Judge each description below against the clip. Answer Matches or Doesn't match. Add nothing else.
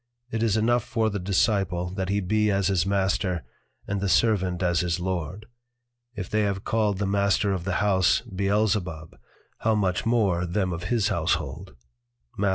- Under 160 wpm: Doesn't match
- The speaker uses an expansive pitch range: Doesn't match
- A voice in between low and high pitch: Doesn't match